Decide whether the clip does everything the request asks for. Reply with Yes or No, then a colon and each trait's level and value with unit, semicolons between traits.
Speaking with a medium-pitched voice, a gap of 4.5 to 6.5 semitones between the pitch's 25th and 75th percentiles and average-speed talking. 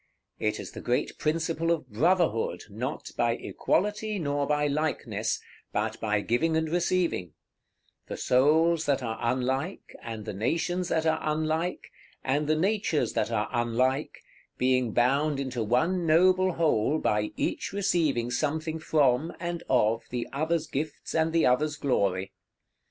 Yes: medium, 150 Hz; average, 5.0 semitones; average, 145 wpm